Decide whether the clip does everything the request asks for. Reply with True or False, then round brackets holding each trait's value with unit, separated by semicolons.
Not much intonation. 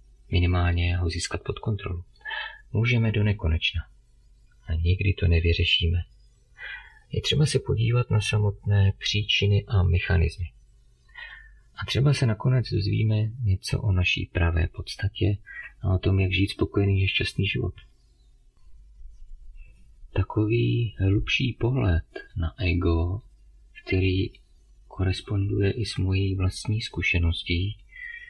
False (4.1 semitones)